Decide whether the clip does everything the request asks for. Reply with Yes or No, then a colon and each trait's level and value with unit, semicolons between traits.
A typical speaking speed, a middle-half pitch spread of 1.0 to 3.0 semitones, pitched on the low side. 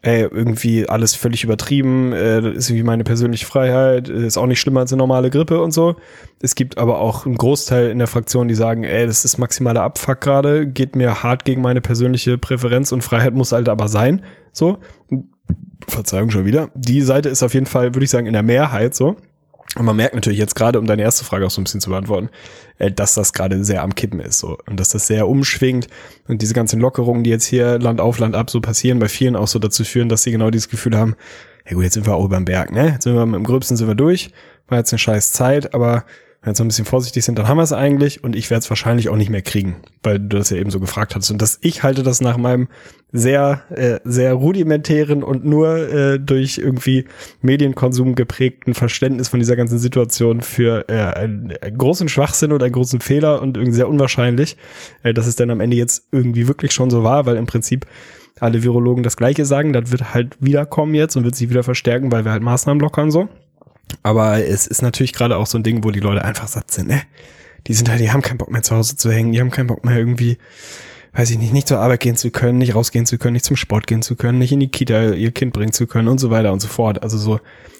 No: fast, 245 wpm; narrow, 2.6 semitones; low, 120 Hz